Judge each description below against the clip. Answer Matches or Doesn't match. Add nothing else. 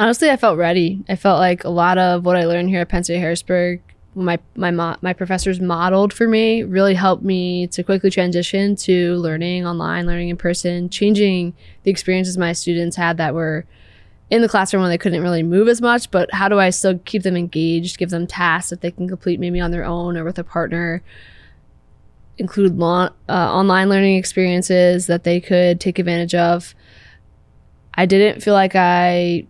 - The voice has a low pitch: Doesn't match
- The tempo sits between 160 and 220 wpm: Matches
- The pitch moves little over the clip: Matches